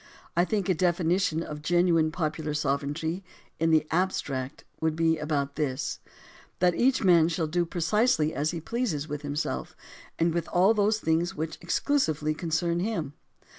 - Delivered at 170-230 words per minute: No, average, 155 wpm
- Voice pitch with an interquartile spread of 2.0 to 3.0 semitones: Yes, average, 2.7 semitones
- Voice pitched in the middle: Yes, medium, 165 Hz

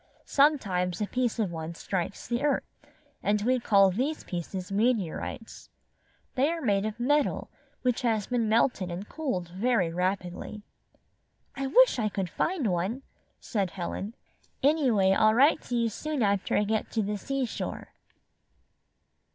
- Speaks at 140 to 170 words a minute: Yes, average, 145 wpm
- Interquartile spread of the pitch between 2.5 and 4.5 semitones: No, average, 5.0 semitones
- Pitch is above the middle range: Yes, high, 215 Hz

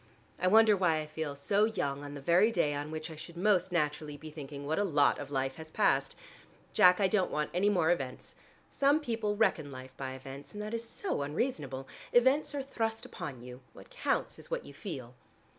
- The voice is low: No, medium, 160 Hz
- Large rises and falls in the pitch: Yes, wide, 6.8 semitones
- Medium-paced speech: No, fast, 210 wpm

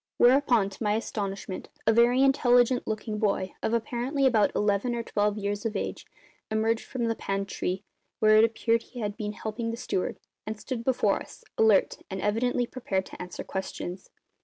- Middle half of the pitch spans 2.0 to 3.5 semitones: Yes, average, 2.7 semitones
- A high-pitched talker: Yes, high, 220 Hz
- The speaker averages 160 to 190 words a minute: Yes, average, 175 wpm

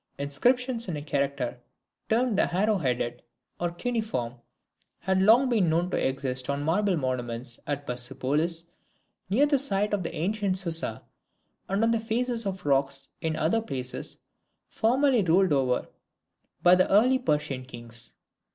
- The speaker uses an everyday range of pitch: No, wide, 8.2 semitones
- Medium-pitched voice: Yes, medium, 170 Hz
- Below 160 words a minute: Yes, average, 150 wpm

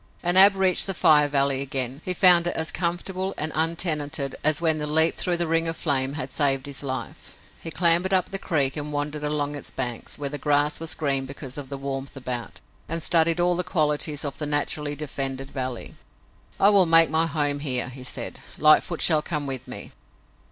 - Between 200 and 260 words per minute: Yes, fast, 205 wpm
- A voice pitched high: No, medium, 150 Hz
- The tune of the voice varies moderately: Yes, average, 3.1 semitones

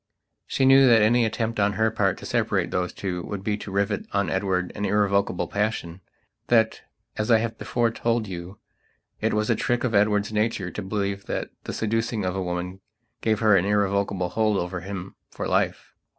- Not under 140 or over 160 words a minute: No, average, 195 wpm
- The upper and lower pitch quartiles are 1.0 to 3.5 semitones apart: Yes, narrow, 2.6 semitones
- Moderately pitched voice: No, low, 105 Hz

